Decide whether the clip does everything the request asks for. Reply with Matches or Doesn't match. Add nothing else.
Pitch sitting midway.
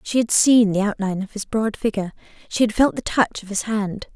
Doesn't match